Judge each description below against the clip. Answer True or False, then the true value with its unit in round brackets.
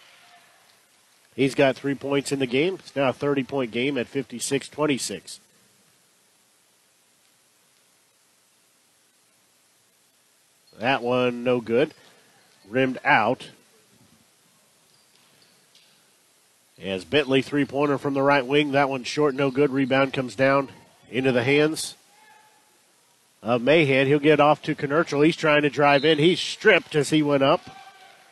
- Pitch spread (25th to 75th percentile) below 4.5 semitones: False (5.0 semitones)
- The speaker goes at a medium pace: False (125 wpm)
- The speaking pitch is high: False (135 Hz)